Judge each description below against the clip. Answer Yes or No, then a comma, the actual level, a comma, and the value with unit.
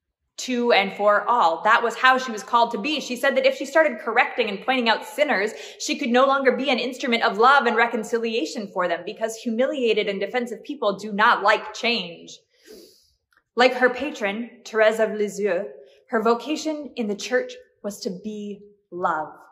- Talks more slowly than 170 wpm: No, average, 185 wpm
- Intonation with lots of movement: No, average, 3.8 semitones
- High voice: Yes, high, 235 Hz